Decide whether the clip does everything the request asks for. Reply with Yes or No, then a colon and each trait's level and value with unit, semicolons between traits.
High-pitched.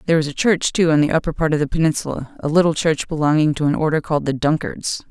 No: medium, 155 Hz